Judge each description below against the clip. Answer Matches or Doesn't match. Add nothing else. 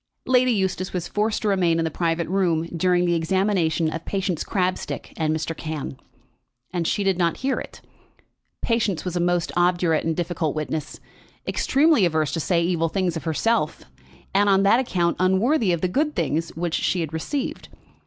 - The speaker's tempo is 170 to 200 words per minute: Matches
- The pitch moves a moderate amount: Matches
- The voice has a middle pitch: Matches